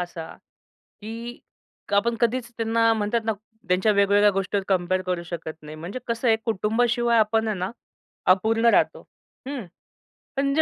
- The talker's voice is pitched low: No, high, 220 Hz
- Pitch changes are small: No, average, 3.8 semitones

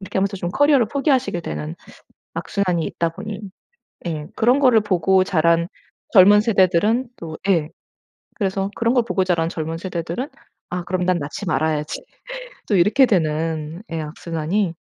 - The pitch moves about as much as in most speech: Yes, average, 4.2 semitones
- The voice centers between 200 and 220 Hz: No, medium, 185 Hz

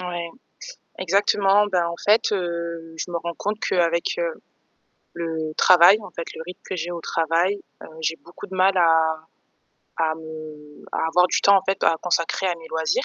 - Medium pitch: Yes, medium, 170 Hz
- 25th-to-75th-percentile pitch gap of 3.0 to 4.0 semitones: No, narrow, 2.6 semitones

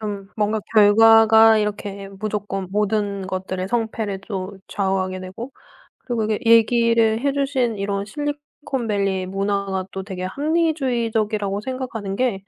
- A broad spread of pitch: No, average, 2.8 semitones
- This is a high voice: Yes, high, 210 Hz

